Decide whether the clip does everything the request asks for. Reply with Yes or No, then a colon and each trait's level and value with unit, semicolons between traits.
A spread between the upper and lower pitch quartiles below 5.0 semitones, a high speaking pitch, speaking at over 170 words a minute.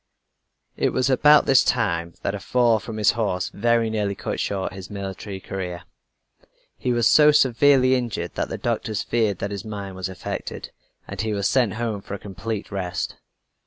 No: average, 3.5 semitones; low, 105 Hz; average, 180 wpm